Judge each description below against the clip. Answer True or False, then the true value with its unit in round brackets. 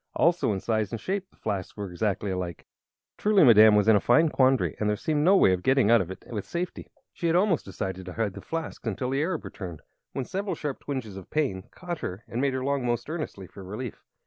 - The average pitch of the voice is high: False (120 Hz)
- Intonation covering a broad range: True (7.8 semitones)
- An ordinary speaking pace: False (240 wpm)